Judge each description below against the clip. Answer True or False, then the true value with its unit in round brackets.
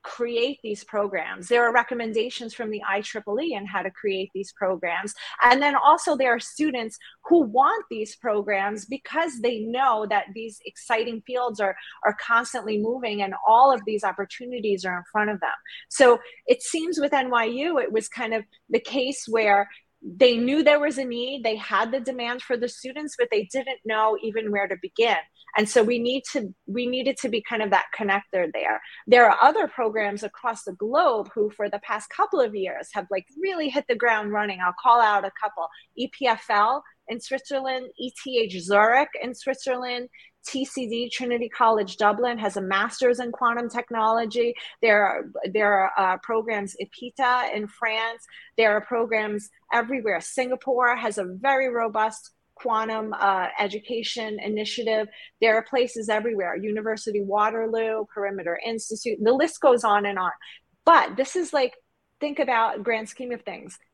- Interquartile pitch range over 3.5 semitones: False (3.0 semitones)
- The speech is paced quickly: False (175 wpm)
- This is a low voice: False (230 Hz)